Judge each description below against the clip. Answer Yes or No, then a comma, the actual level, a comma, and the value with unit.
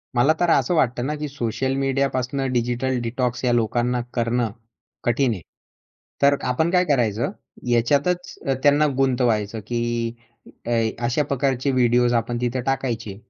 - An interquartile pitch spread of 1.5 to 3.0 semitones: Yes, narrow, 2.6 semitones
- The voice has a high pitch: No, low, 125 Hz